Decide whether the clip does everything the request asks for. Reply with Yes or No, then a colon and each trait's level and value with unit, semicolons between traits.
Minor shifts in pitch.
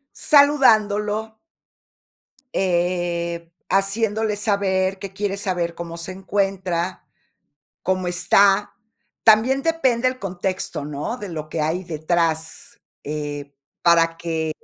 No: average, 3.6 semitones